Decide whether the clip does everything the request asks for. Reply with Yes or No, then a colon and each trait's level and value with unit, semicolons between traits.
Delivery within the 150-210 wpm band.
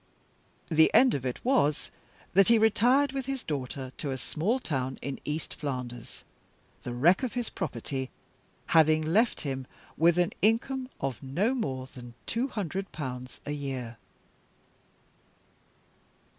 No: average, 140 wpm